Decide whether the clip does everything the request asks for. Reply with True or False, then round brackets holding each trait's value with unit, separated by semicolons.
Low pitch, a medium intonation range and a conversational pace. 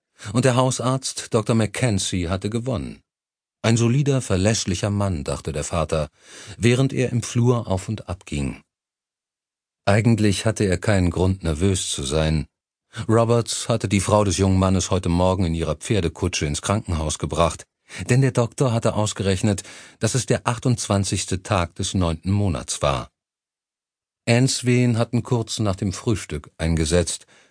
True (100 Hz; 4.8 semitones; 145 wpm)